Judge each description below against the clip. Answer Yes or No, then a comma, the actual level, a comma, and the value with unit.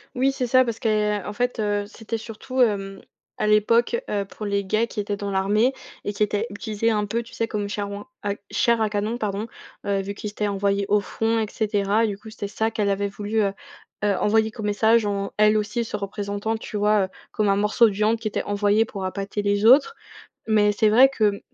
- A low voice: No, high, 210 Hz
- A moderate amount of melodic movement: No, narrow, 1.7 semitones